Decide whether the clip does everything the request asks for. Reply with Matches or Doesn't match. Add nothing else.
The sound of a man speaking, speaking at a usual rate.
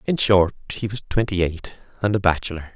Matches